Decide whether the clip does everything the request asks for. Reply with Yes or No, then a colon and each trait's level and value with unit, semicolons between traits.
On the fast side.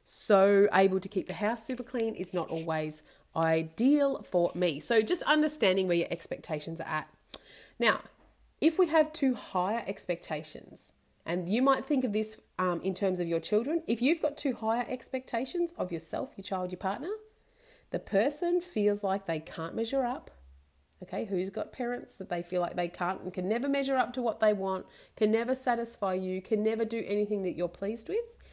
No: average, 195 wpm